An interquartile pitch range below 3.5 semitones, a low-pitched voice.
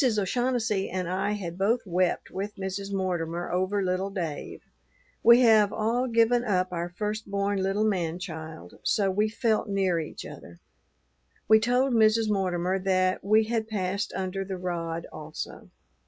No: average, 3.0 semitones; high, 195 Hz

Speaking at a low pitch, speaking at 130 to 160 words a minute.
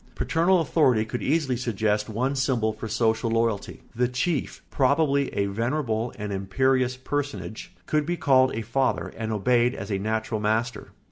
Yes: low, 120 Hz; average, 155 wpm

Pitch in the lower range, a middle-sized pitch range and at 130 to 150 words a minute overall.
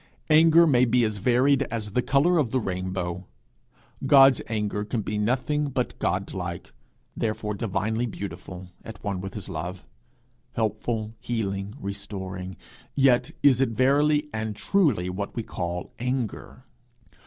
Yes: low, 110 Hz; average, 4.9 semitones; slow, 135 wpm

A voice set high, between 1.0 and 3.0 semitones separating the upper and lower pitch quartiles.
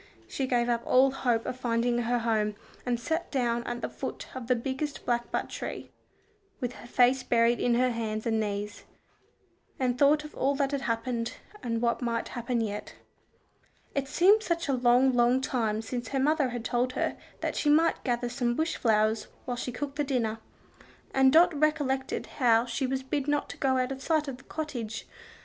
Yes: very high, 250 Hz; narrow, 2.5 semitones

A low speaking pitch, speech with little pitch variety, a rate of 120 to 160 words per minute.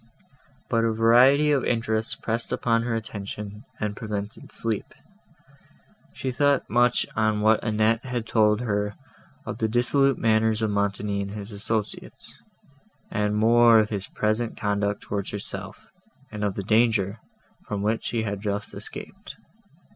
Yes: low, 110 Hz; narrow, 2.1 semitones; average, 145 wpm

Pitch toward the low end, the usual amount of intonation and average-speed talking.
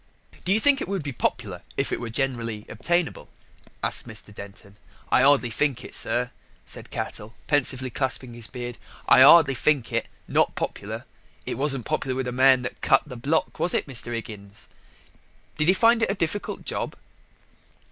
Yes: low, 130 Hz; average, 4.3 semitones; average, 180 wpm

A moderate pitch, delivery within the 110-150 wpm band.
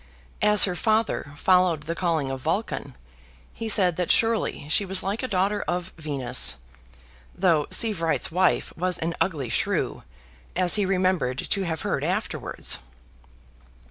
Yes: medium, 180 Hz; average, 140 wpm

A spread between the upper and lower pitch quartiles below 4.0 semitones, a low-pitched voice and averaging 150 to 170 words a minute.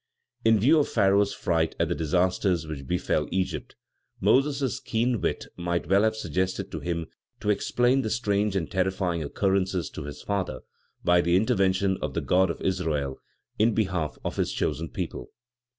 Yes: average, 3.6 semitones; very low, 95 Hz; average, 165 wpm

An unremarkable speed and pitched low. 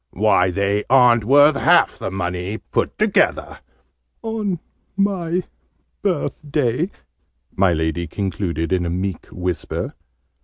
No: slow, 110 wpm; low, 105 Hz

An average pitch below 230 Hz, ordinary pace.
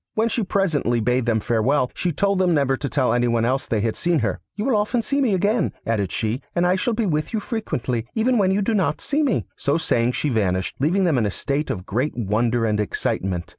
No: medium, 140 Hz; fast, 245 wpm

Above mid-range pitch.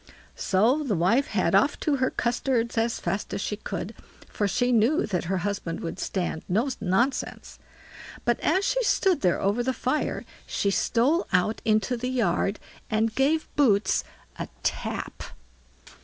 Yes: high, 225 Hz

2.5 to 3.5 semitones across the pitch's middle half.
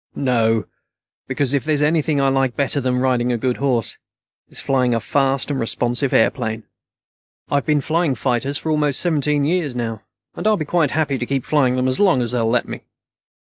Yes: average, 3.2 semitones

